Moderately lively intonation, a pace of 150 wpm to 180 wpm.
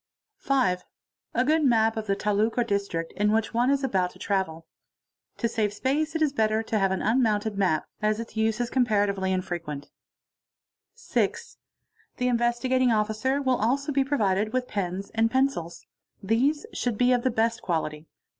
Yes: average, 4.2 semitones; average, 170 wpm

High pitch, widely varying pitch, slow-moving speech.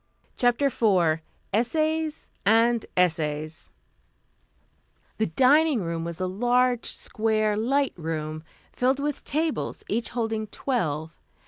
Yes: high, 225 Hz; wide, 7.2 semitones; slow, 105 wpm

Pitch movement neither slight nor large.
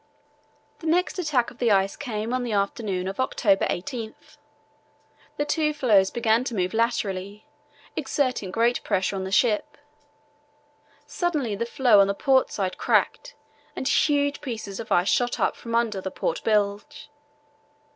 Yes: average, 4.7 semitones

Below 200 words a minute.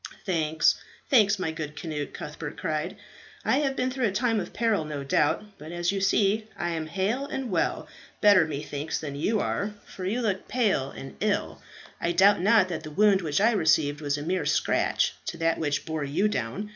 No: fast, 205 wpm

